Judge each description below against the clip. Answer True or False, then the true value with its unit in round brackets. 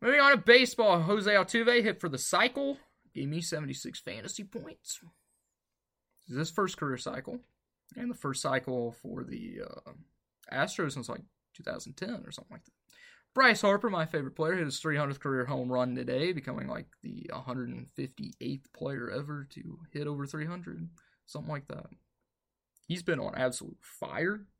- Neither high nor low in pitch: True (160 Hz)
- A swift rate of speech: False (160 wpm)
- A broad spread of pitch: True (7.7 semitones)